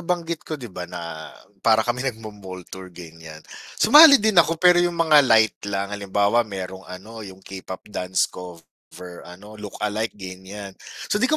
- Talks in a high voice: No, low, 100 Hz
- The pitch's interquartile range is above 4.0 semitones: Yes, average, 5.3 semitones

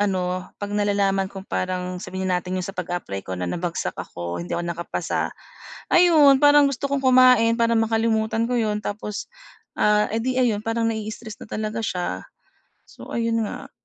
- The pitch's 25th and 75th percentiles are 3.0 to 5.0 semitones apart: Yes, average, 4.0 semitones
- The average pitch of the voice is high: Yes, high, 210 Hz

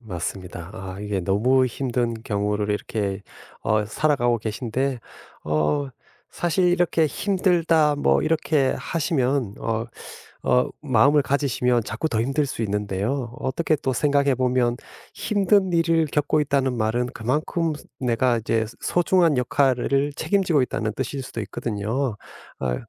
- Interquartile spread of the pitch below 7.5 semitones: Yes, average, 5.2 semitones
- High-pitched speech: No, low, 130 Hz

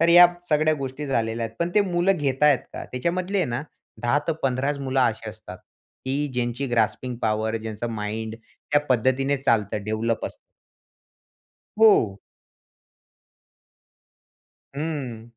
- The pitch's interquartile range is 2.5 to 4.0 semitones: No, average, 4.6 semitones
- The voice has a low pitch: Yes, low, 130 Hz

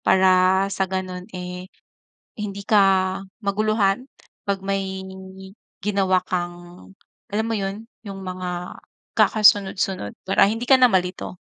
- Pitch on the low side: No, high, 190 Hz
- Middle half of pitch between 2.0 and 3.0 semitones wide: No, narrow, 1.6 semitones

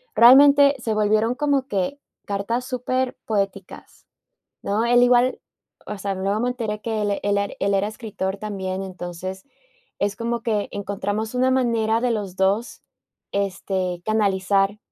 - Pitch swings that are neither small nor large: Yes, average, 3.5 semitones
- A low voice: No, high, 210 Hz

